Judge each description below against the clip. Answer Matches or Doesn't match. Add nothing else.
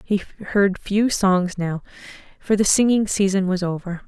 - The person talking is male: Doesn't match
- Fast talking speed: Doesn't match